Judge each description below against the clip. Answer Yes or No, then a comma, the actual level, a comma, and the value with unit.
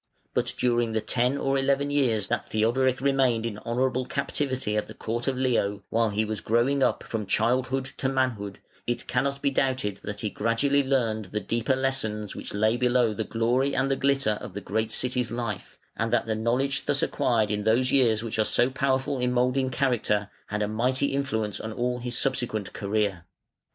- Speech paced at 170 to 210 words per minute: Yes, average, 190 wpm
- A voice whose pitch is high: No, low, 120 Hz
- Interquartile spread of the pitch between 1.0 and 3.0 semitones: No, average, 3.4 semitones